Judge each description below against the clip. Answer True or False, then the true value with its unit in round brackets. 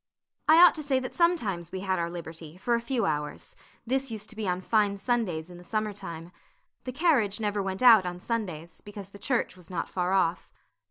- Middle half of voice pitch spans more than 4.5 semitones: True (4.9 semitones)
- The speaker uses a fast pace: True (215 wpm)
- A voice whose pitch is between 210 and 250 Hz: False (200 Hz)